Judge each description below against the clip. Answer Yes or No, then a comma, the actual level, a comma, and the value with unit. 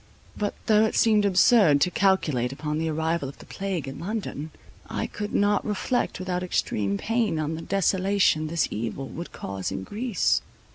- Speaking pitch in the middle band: Yes, medium, 180 Hz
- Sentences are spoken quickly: No, average, 175 wpm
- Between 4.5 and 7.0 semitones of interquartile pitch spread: Yes, wide, 5.4 semitones